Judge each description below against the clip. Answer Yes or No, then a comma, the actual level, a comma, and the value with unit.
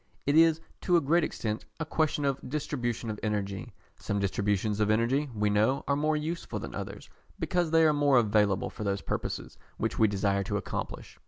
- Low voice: Yes, low, 120 Hz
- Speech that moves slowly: No, average, 190 wpm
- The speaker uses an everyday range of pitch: No, wide, 6.6 semitones